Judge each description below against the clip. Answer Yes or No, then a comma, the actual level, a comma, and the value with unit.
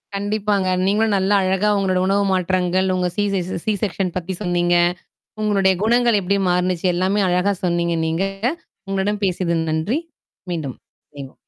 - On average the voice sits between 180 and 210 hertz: Yes, high, 190 Hz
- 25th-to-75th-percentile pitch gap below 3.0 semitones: Yes, narrow, 2.4 semitones